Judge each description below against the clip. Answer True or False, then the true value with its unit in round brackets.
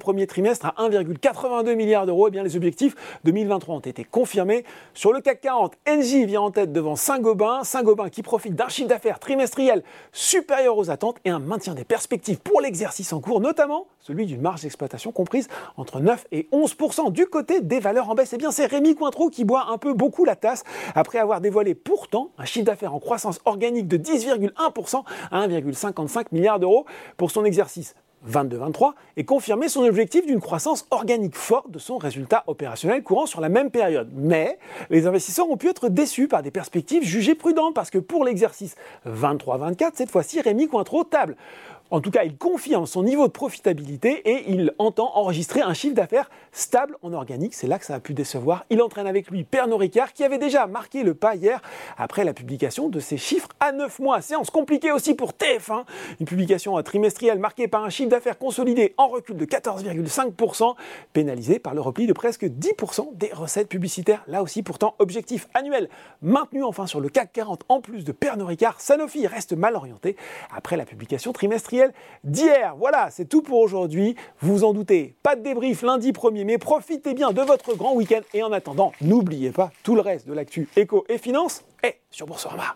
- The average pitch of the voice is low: False (225 Hz)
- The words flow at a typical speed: True (195 wpm)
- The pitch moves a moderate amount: False (6.2 semitones)